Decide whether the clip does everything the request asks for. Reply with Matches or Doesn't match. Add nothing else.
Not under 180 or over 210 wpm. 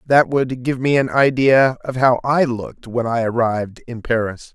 Matches